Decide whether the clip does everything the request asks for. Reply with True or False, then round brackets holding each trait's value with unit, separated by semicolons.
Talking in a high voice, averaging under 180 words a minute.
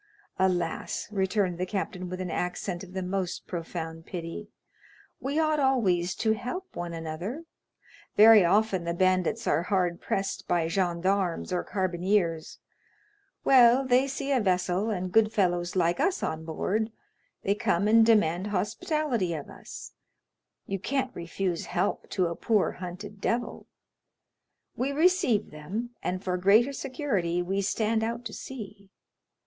True (195 Hz; 145 wpm)